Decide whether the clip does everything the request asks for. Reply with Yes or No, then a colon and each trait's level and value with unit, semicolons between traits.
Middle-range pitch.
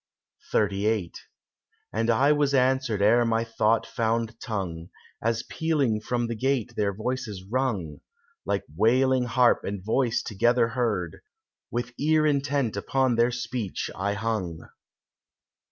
No: low, 115 Hz